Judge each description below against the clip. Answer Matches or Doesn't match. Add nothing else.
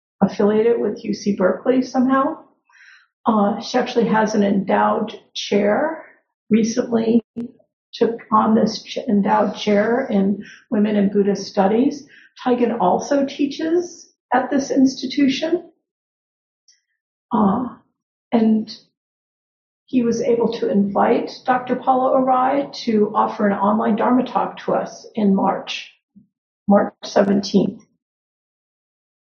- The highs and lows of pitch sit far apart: Doesn't match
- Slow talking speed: Matches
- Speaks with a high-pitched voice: Matches